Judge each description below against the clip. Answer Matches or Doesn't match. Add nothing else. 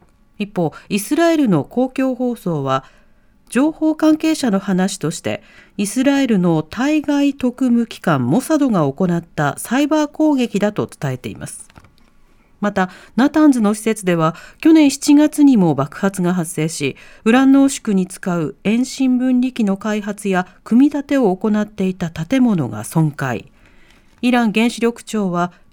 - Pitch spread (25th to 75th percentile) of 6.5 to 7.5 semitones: Matches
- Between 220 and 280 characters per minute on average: Matches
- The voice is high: Matches